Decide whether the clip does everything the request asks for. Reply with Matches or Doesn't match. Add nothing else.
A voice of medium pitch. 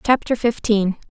Doesn't match